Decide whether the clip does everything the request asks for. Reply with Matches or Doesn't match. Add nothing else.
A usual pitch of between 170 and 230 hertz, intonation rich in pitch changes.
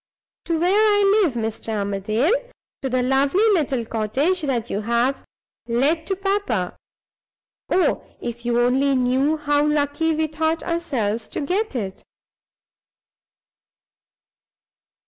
Doesn't match